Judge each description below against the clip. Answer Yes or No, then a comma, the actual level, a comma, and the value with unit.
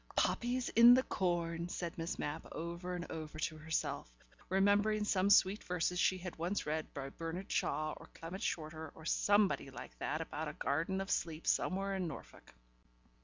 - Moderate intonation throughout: Yes, average, 3.4 semitones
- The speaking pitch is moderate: Yes, medium, 175 Hz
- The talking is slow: No, average, 170 wpm